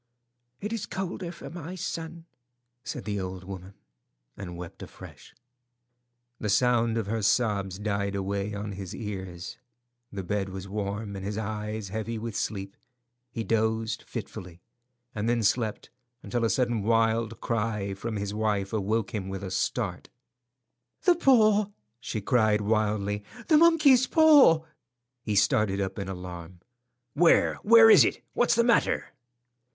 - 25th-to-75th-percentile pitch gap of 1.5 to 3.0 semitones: No, average, 3.5 semitones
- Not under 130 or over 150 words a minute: Yes, average, 145 wpm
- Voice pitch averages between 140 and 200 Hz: No, low, 105 Hz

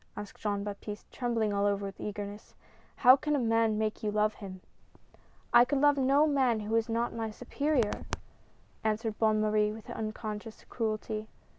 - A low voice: No, high, 220 Hz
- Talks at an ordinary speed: Yes, average, 180 wpm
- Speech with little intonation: Yes, narrow, 2.2 semitones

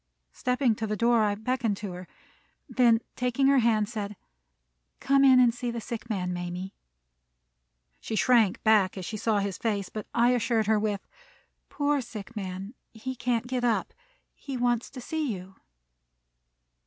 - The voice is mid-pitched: No, high, 225 Hz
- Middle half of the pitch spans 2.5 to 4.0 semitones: Yes, average, 3.3 semitones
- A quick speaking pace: No, average, 165 wpm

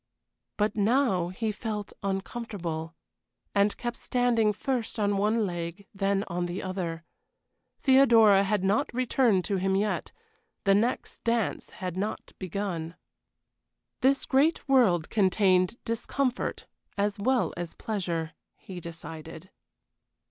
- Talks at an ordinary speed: No, slow, 120 wpm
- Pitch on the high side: Yes, high, 200 Hz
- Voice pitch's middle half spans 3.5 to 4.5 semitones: Yes, average, 4.0 semitones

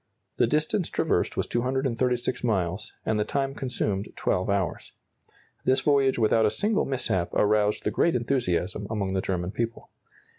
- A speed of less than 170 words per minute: Yes, average, 150 wpm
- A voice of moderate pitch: No, low, 115 Hz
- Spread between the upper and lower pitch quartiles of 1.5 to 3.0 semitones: No, average, 4.9 semitones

